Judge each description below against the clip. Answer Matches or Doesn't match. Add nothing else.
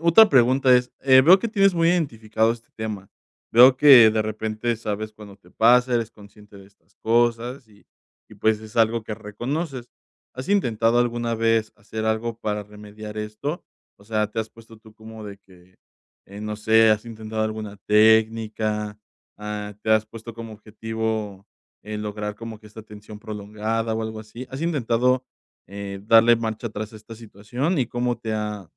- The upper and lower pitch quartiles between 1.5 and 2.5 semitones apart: Matches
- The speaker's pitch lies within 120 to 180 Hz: Doesn't match